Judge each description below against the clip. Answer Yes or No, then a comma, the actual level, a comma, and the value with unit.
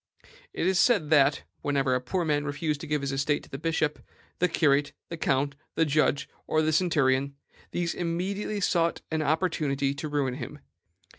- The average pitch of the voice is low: No, medium, 150 Hz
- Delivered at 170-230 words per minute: Yes, average, 175 wpm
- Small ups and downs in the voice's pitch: No, average, 3.1 semitones